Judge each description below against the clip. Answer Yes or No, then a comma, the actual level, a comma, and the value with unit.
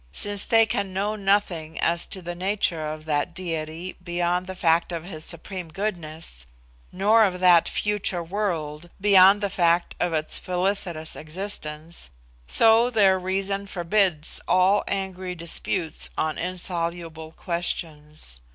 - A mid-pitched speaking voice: Yes, medium, 180 Hz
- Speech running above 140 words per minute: No, slow, 135 wpm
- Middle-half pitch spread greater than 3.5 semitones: No, average, 3.2 semitones